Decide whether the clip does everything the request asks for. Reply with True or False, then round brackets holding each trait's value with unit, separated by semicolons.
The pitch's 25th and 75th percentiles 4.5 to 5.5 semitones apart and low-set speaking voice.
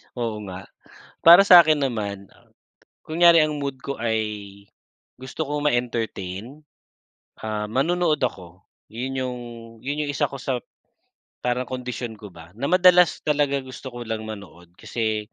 True (5.2 semitones; 125 Hz)